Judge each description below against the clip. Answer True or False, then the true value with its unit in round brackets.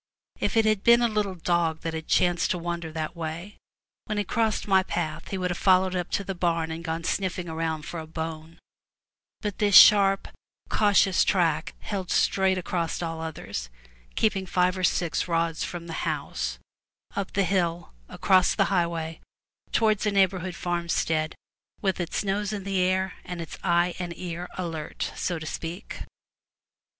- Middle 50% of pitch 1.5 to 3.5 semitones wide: True (2.7 semitones)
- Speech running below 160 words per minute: False (175 wpm)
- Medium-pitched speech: True (175 Hz)